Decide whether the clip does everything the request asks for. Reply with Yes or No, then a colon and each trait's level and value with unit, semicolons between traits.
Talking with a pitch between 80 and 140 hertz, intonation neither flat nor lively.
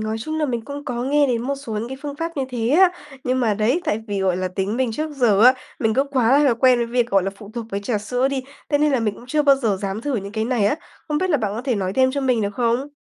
No: high, 245 Hz; average, 4.3 semitones